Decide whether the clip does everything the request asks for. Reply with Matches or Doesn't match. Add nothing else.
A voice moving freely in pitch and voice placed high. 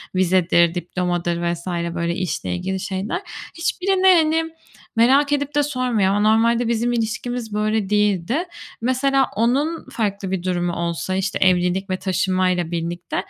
Matches